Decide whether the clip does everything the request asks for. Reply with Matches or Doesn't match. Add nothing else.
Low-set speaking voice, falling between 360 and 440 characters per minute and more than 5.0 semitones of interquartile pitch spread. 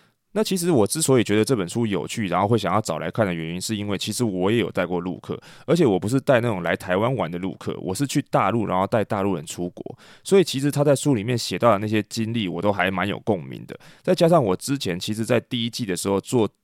Matches